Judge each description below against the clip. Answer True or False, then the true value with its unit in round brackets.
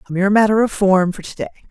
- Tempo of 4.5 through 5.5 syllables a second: False (7.8 syllables/s)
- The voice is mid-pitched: False (200 Hz)